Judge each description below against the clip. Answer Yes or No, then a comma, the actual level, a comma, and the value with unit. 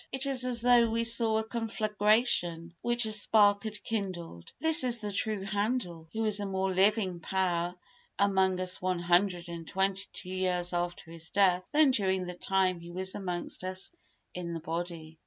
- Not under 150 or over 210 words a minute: Yes, average, 180 wpm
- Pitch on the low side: No, high, 190 Hz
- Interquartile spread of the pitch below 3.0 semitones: No, average, 3.6 semitones